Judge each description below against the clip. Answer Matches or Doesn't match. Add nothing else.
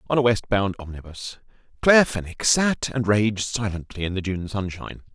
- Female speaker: Doesn't match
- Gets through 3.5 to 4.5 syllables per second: Doesn't match